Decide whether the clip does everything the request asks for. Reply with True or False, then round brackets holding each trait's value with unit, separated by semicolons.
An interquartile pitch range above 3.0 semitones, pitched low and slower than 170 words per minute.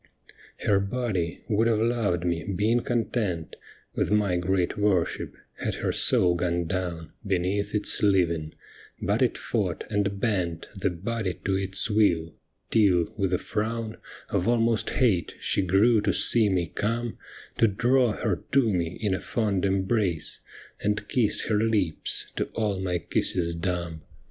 True (3.8 semitones; 100 Hz; 150 wpm)